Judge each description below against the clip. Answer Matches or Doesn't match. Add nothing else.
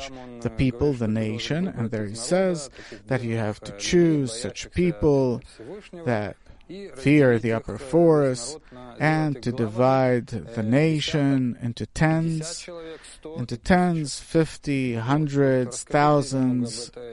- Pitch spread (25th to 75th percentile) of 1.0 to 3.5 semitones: Doesn't match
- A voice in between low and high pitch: Doesn't match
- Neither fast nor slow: Doesn't match